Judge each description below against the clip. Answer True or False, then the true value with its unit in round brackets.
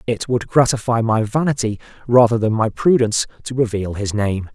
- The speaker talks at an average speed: True (170 wpm)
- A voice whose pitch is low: True (115 Hz)